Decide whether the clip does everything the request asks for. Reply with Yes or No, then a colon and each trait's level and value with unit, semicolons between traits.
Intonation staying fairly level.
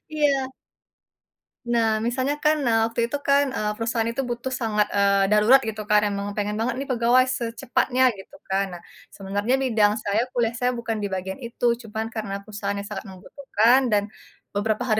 No: average, 3.1 semitones